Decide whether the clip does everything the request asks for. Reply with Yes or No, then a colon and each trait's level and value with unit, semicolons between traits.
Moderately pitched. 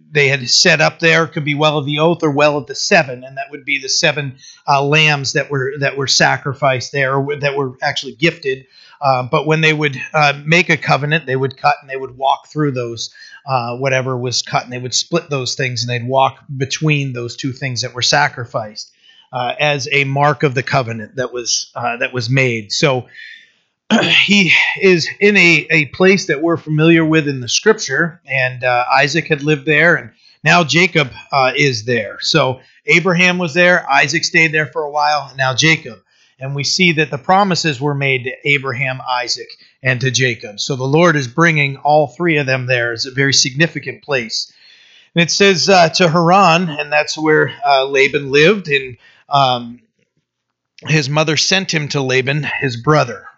Yes: medium, 145 Hz